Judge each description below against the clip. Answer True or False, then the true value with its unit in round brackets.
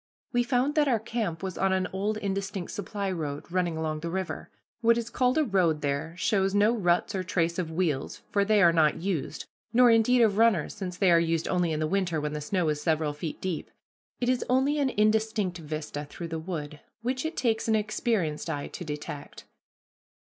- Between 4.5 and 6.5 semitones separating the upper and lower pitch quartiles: True (5.4 semitones)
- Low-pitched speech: False (185 Hz)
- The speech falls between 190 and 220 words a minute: True (205 wpm)